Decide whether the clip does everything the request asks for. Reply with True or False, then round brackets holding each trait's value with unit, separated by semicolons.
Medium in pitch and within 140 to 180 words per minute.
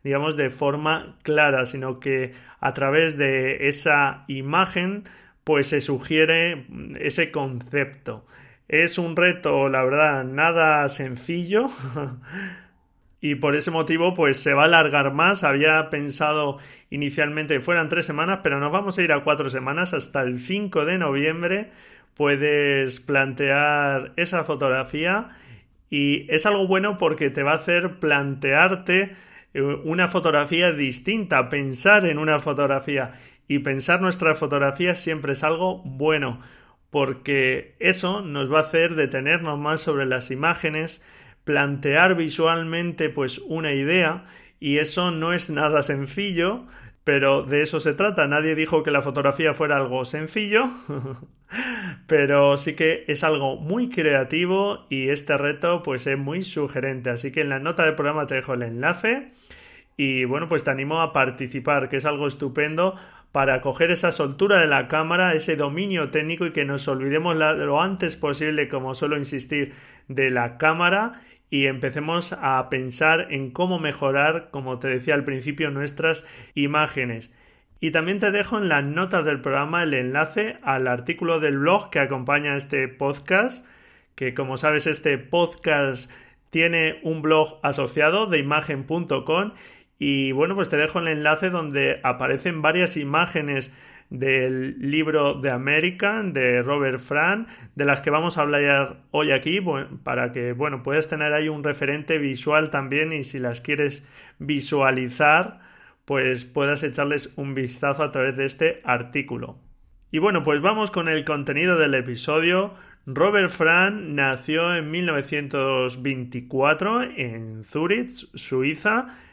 True (150 Hz; 145 wpm)